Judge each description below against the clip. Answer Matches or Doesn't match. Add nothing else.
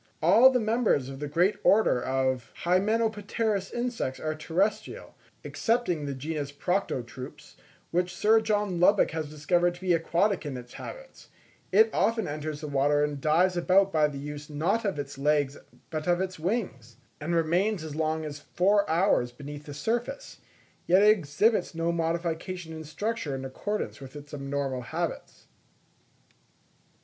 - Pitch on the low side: Doesn't match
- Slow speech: Doesn't match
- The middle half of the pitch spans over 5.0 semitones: Matches